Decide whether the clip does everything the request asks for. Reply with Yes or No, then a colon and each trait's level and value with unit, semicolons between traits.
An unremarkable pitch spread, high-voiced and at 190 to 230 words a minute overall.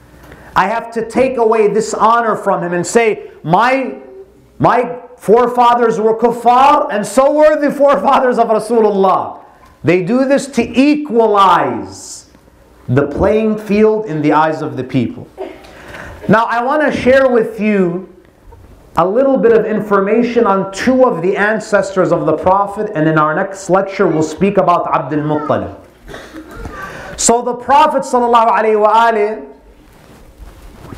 No: average, 4.3 semitones; high, 215 Hz; slow, 135 wpm